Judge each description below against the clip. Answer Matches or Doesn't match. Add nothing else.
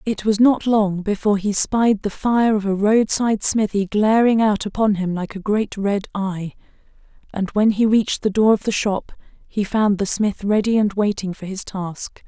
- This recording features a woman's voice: Matches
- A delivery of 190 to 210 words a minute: Matches